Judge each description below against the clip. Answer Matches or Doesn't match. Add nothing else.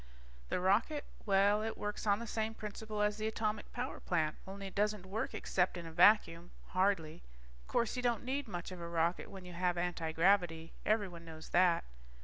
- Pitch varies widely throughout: Doesn't match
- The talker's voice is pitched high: Matches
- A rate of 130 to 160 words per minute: Doesn't match